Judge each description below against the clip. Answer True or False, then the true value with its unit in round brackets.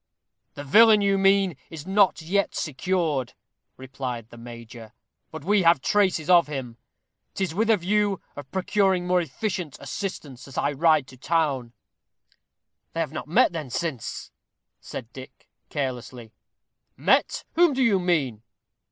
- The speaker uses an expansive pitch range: True (6.5 semitones)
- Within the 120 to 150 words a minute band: True (145 wpm)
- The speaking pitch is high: False (160 Hz)